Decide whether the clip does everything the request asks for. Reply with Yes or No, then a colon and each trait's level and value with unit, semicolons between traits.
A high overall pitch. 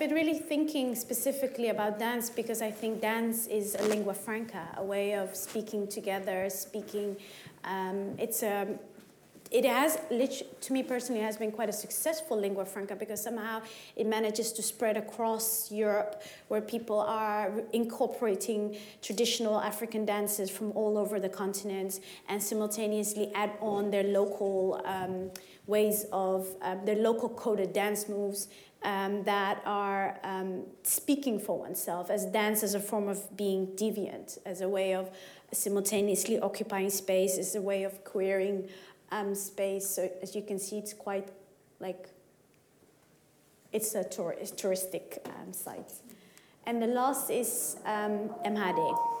Yes: high, 210 Hz